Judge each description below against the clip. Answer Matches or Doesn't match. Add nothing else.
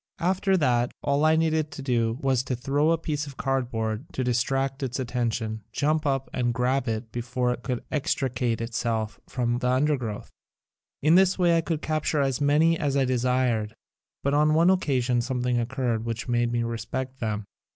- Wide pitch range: Doesn't match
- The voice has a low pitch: Matches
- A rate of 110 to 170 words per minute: Doesn't match